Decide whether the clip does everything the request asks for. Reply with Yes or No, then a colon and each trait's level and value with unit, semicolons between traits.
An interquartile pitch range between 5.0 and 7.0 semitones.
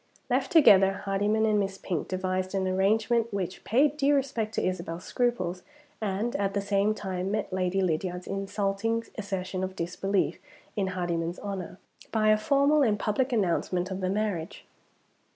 No: average, 2.7 semitones